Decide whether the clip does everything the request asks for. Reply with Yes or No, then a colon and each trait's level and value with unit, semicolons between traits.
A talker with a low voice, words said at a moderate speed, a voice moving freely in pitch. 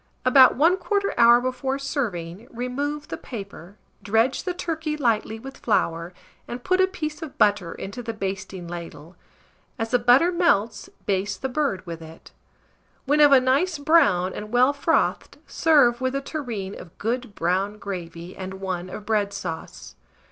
No: high, 235 Hz; average, 160 wpm; wide, 6.6 semitones